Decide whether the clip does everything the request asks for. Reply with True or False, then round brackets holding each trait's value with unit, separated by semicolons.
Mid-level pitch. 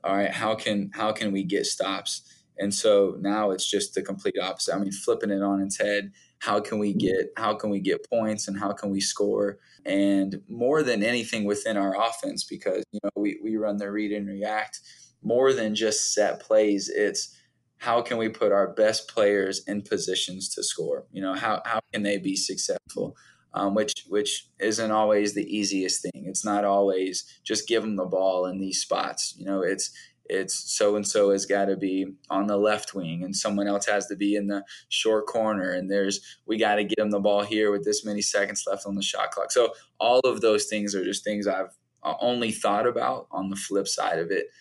False (100 Hz)